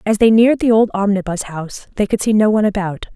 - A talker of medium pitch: No, high, 205 Hz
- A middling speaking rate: No, fast, 245 wpm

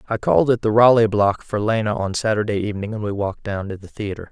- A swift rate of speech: Yes, fast, 250 wpm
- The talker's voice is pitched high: No, low, 105 Hz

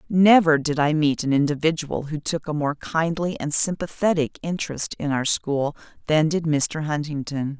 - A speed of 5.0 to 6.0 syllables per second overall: No, 4.7 syllables/s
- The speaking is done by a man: No, female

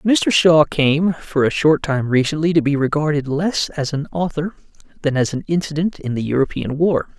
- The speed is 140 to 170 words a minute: No, average, 190 wpm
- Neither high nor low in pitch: Yes, medium, 150 Hz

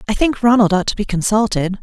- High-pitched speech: Yes, high, 210 Hz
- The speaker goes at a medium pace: No, fast, 230 wpm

